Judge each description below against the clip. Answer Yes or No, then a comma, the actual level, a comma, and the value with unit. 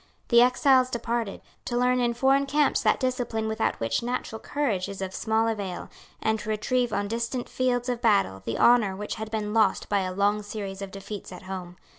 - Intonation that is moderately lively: Yes, average, 3.6 semitones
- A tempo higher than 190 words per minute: Yes, average, 200 wpm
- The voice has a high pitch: Yes, high, 220 Hz